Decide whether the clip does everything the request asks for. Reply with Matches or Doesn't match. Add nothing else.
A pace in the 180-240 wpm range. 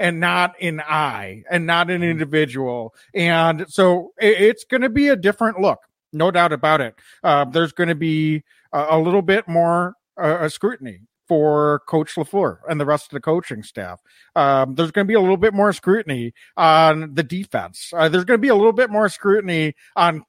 Matches